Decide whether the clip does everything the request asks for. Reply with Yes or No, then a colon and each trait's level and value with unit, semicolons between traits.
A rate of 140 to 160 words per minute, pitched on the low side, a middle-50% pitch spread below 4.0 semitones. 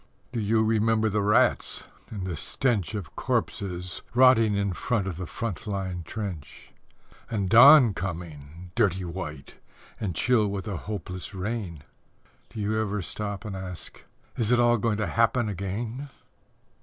Yes: average, 150 wpm; low, 100 Hz; average, 3.5 semitones